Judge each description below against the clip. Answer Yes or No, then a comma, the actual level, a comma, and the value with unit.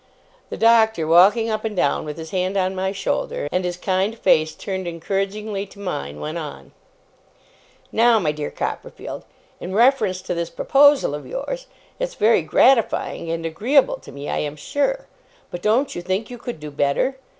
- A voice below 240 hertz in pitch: Yes, high, 190 Hz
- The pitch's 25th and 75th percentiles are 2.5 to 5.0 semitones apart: No, wide, 5.6 semitones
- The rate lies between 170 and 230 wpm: Yes, average, 175 wpm